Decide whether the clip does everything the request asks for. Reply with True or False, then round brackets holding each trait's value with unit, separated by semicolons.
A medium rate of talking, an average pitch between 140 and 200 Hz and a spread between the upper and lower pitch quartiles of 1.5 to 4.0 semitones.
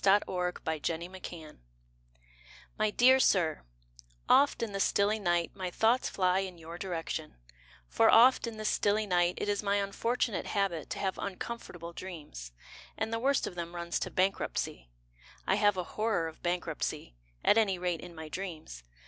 True (165 wpm; 185 Hz; 3.5 semitones)